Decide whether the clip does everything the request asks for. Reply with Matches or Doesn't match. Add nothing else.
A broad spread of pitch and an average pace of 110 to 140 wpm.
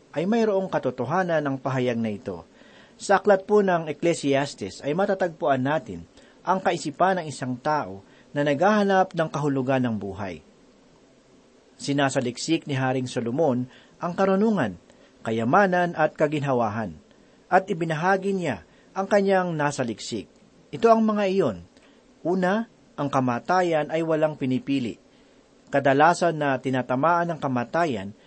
Matches